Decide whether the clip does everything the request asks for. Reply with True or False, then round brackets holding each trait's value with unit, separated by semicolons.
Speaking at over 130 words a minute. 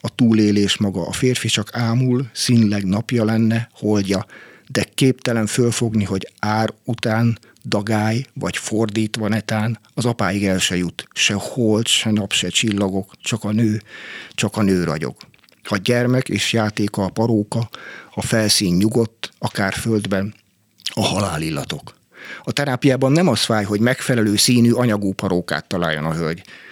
True (150 wpm)